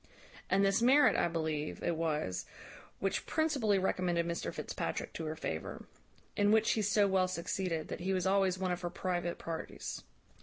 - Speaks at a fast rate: No, average, 175 wpm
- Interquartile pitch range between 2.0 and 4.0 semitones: Yes, average, 2.9 semitones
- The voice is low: No, medium, 185 Hz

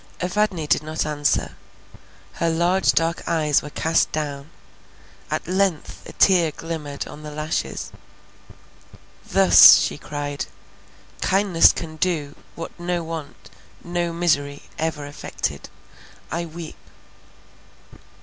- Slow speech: Yes, slow, 110 wpm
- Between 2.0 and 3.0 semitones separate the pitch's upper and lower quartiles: Yes, narrow, 2.6 semitones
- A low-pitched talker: No, medium, 160 Hz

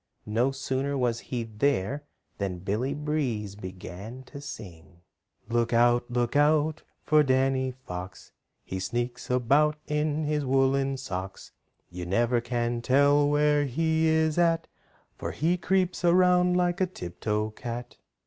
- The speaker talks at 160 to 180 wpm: No, average, 140 wpm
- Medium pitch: No, low, 130 Hz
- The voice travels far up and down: No, average, 4.6 semitones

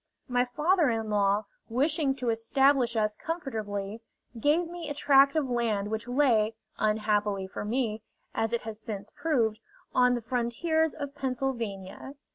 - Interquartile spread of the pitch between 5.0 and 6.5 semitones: No, average, 4.5 semitones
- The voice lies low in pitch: No, high, 240 Hz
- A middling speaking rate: Yes, average, 145 wpm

